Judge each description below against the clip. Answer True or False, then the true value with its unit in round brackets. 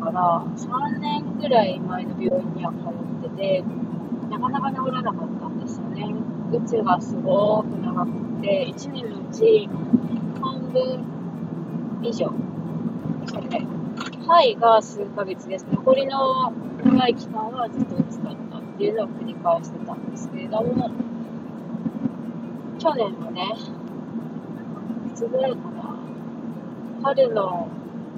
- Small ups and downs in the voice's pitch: True (2.1 semitones)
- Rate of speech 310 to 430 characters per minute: False (220 characters per minute)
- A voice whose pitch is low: False (230 Hz)